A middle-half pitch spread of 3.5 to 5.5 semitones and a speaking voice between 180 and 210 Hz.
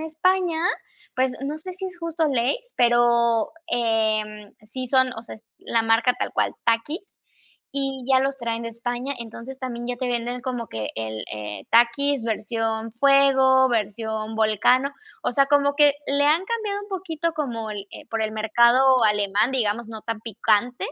No: average, 3.8 semitones; high, 240 Hz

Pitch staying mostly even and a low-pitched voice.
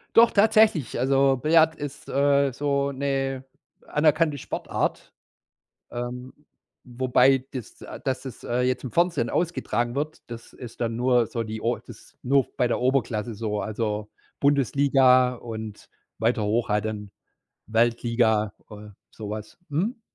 No: average, 3.5 semitones; low, 125 Hz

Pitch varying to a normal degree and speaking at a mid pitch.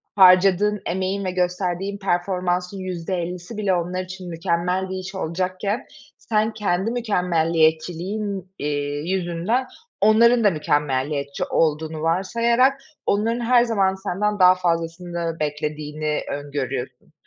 Yes: average, 3.4 semitones; medium, 180 Hz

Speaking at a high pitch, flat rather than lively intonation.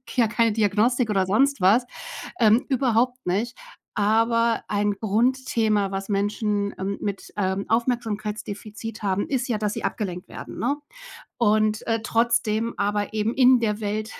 Yes: high, 215 Hz; narrow, 2.2 semitones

